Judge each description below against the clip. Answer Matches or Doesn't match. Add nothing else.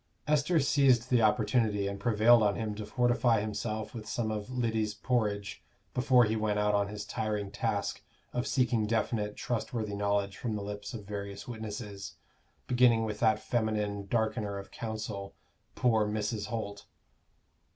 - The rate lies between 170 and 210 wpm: Doesn't match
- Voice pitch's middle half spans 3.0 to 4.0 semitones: Doesn't match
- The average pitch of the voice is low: Matches